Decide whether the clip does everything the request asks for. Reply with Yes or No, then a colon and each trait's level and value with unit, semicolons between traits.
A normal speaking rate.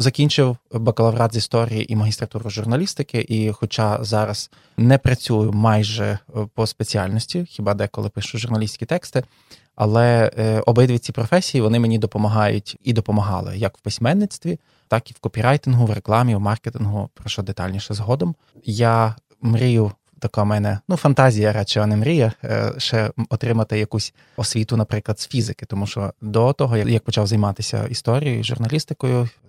Yes: average, 140 wpm